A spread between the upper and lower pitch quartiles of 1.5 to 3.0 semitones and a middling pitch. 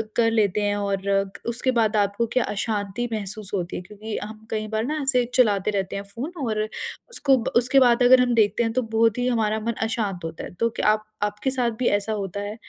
No: average, 2.7 semitones; high, 220 Hz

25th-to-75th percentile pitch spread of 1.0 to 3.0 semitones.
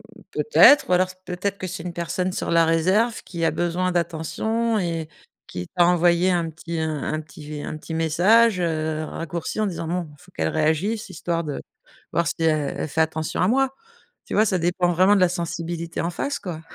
Yes: narrow, 2.4 semitones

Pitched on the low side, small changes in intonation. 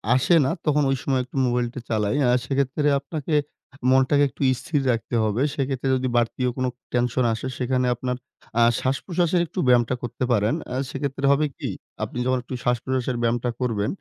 Yes: low, 130 Hz; narrow, 2.2 semitones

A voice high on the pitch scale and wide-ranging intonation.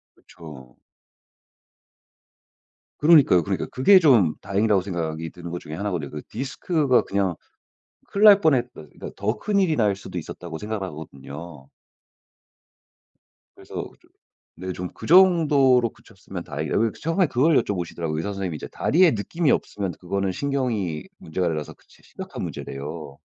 No: low, 100 Hz; wide, 8.7 semitones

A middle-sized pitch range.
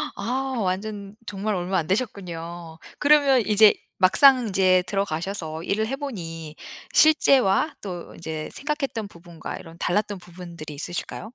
Yes: average, 4.6 semitones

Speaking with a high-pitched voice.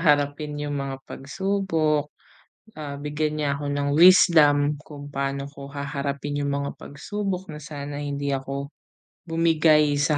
No: medium, 145 Hz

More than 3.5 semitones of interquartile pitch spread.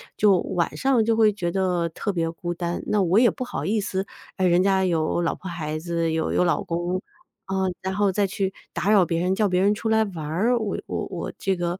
No: average, 3.0 semitones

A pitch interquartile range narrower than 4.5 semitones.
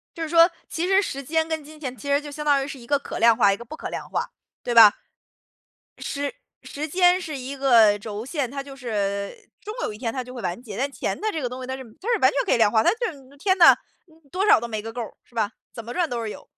No: average, 5.2 semitones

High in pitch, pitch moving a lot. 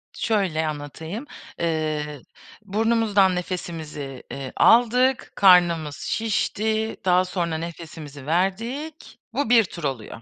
No: medium, 180 Hz; wide, 6.0 semitones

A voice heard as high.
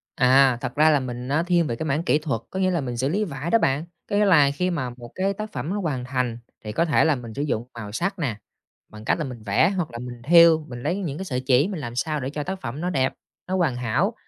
No: medium, 145 Hz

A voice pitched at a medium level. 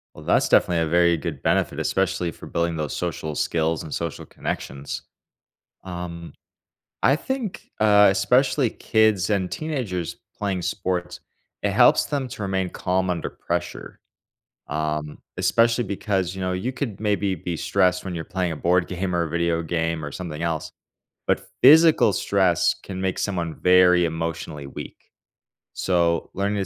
No: very low, 90 Hz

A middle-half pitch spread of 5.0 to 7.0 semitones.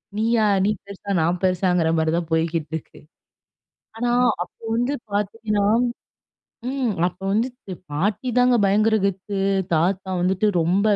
No: average, 4.0 semitones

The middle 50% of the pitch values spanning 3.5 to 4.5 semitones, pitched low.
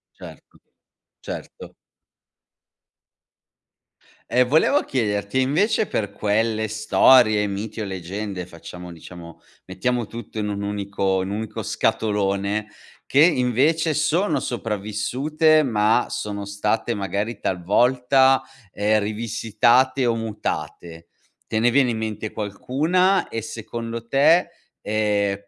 Yes: average, 3.8 semitones; low, 110 Hz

